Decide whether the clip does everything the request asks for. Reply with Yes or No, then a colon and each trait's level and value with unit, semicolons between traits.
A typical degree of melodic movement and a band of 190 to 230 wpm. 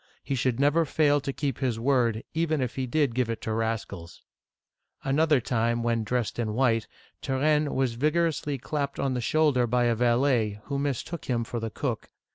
Yes: average, 3.6 semitones; average, 195 wpm